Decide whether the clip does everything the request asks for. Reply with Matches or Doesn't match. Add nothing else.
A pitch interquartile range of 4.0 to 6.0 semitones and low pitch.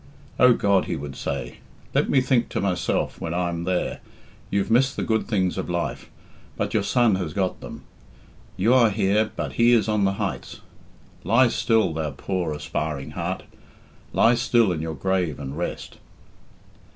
Matches